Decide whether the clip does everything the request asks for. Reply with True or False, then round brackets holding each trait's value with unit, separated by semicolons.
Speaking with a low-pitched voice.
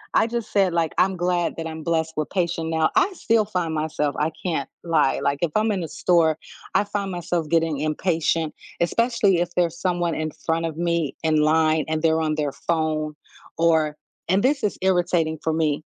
False (165 Hz)